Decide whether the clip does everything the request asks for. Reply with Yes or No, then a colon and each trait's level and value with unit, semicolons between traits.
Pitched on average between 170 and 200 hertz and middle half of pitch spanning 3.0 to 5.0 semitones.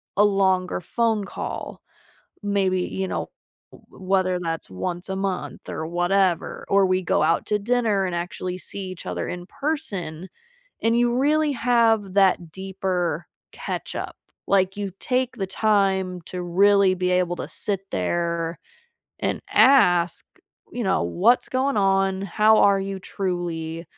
No: high, 190 Hz; narrow, 2.5 semitones